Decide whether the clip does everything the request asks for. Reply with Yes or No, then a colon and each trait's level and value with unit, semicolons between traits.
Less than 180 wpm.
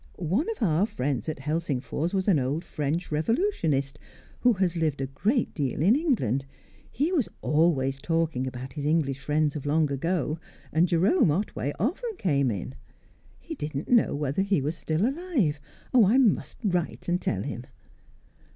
Yes: average, 165 wpm